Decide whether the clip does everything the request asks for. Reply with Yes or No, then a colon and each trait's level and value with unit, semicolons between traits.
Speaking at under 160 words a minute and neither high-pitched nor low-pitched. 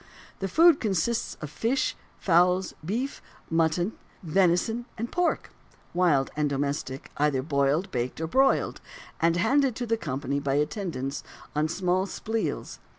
Yes: average, 140 wpm; medium, 175 Hz